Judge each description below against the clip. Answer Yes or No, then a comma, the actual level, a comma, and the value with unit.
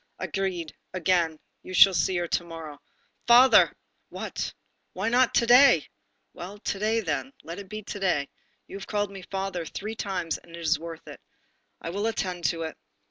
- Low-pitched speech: No, medium, 185 Hz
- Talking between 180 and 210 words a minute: Yes, average, 185 wpm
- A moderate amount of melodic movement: Yes, average, 3.6 semitones